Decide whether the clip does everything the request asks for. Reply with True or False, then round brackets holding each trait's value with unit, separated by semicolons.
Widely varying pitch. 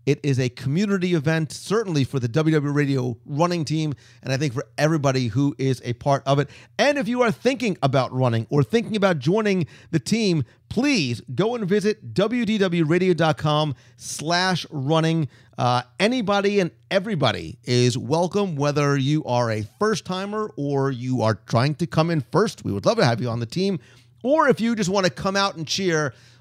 True (7.2 semitones)